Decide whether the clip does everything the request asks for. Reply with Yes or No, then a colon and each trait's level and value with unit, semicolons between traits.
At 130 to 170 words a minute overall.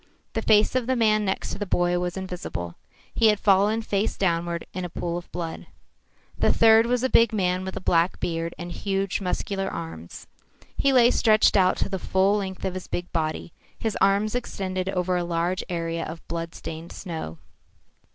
No: average, 190 wpm